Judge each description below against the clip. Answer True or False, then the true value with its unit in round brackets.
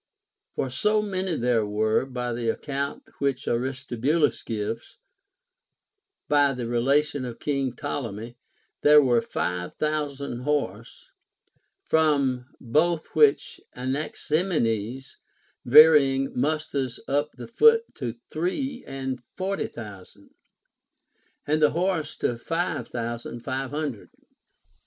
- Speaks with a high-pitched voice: False (135 Hz)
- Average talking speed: False (105 wpm)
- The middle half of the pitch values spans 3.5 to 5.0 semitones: True (4.2 semitones)